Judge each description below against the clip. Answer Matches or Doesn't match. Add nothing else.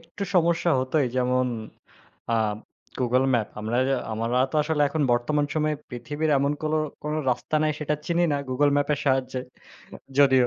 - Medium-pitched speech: Matches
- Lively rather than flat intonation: Doesn't match